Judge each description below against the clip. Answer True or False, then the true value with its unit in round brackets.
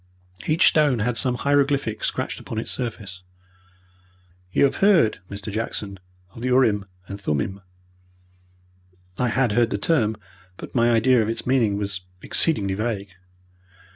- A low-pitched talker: True (115 Hz)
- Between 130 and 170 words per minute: True (140 wpm)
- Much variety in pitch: False (4.1 semitones)